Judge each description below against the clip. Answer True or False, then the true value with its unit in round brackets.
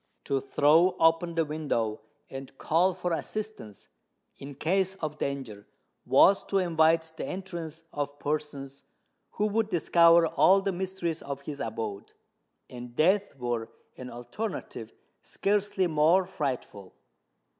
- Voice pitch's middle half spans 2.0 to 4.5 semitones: False (5.2 semitones)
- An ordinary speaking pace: False (125 wpm)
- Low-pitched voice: False (160 Hz)